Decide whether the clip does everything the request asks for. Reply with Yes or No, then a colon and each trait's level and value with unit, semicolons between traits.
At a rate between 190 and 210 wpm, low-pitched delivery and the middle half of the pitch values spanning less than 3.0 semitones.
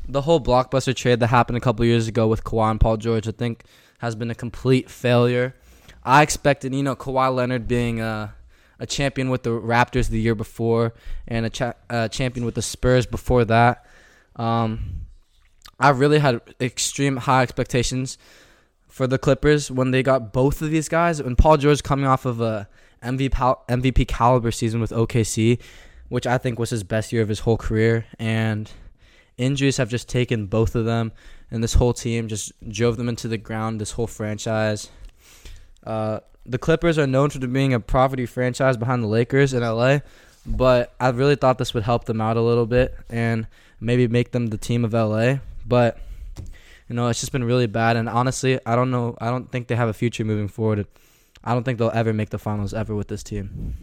Yes: average, 200 wpm; low, 120 Hz; narrow, 2.4 semitones